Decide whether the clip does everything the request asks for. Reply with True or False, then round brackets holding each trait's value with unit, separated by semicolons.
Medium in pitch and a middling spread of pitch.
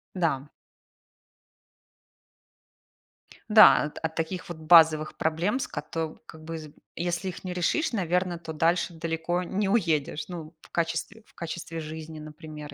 False (165 Hz; 2.1 semitones)